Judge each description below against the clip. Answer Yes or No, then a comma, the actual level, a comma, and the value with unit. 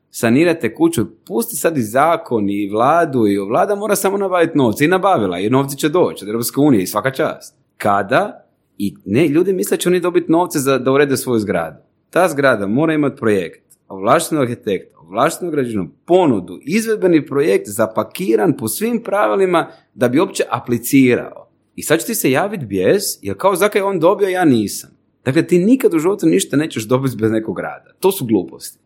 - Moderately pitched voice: Yes, medium, 150 Hz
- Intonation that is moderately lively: No, wide, 8.1 semitones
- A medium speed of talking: No, fast, 185 wpm